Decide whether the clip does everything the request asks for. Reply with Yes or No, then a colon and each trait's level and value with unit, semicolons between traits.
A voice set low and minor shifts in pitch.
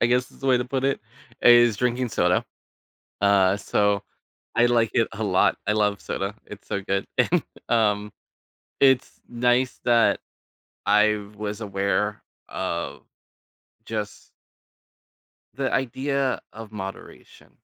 No: low, 110 Hz; average, 3.4 semitones